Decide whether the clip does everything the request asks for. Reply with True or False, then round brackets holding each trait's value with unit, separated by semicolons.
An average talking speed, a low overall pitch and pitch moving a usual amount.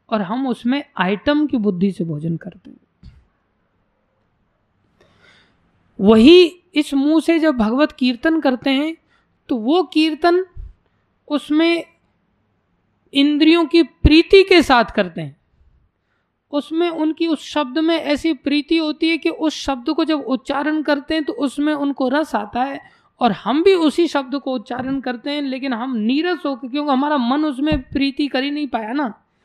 False (155 wpm; 290 Hz; 3.8 semitones)